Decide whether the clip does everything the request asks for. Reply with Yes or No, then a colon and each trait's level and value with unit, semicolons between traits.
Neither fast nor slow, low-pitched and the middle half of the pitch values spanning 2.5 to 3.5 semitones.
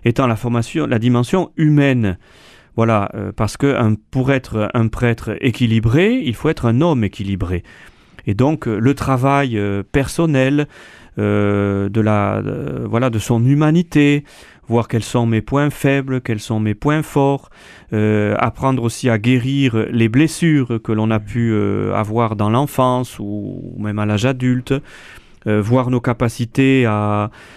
No: average, 155 wpm; low, 120 Hz; average, 4.0 semitones